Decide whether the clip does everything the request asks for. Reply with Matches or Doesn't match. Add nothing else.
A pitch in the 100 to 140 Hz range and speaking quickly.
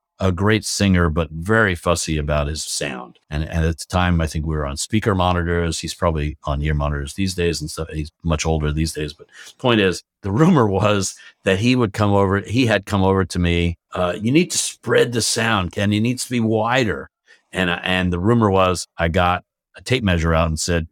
Doesn't match